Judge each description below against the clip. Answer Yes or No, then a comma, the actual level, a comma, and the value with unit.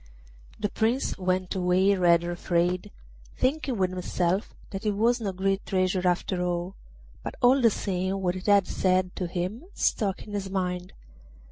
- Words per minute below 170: Yes, average, 160 wpm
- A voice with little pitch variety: Yes, narrow, 2.2 semitones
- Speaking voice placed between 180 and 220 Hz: Yes, medium, 185 Hz